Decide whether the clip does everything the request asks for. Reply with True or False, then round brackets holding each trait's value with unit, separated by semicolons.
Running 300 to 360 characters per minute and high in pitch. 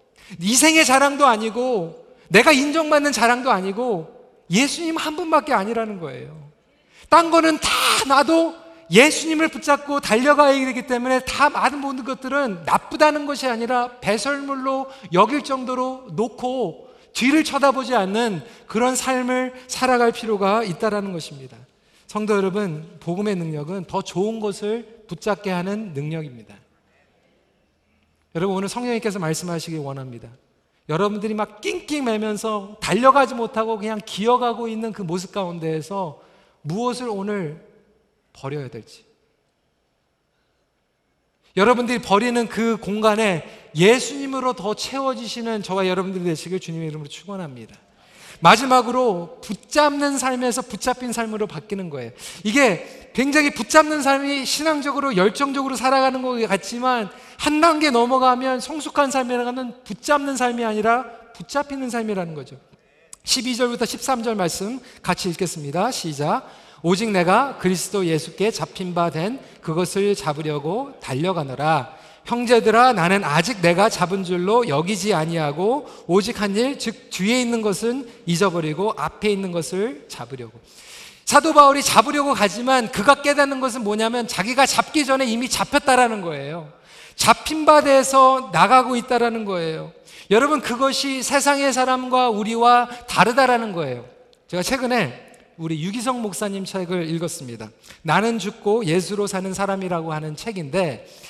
True (315 characters per minute; 225 Hz)